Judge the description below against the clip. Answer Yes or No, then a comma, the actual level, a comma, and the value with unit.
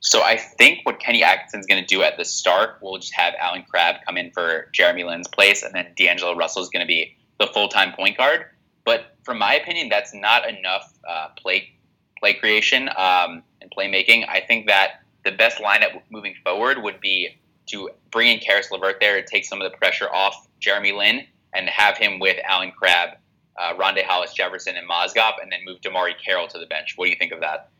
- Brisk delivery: Yes, fast, 215 wpm